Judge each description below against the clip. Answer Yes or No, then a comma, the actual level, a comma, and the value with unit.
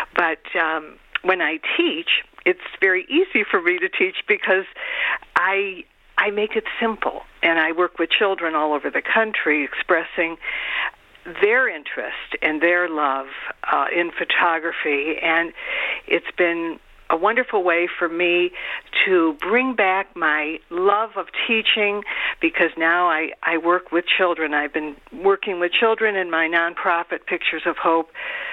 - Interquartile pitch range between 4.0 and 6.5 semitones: Yes, wide, 5.5 semitones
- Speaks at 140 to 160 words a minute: Yes, average, 145 wpm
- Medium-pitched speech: Yes, medium, 180 Hz